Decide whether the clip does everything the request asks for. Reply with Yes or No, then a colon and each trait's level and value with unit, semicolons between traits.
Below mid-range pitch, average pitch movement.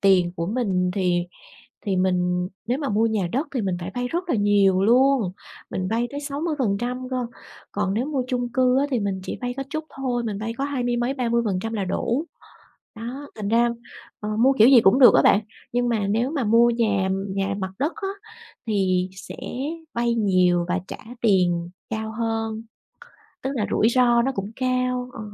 No: high, 230 Hz; average, 4.3 semitones